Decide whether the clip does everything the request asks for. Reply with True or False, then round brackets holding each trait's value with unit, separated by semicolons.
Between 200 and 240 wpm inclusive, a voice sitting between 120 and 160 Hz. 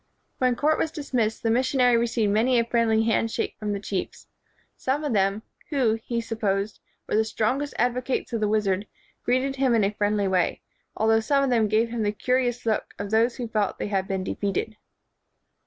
False (205 wpm; 225 Hz)